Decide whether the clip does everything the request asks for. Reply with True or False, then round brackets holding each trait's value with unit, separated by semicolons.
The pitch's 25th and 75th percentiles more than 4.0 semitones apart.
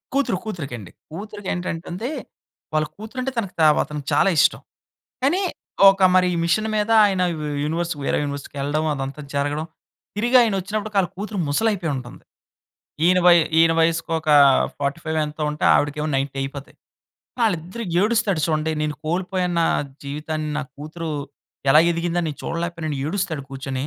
True (4.5 semitones)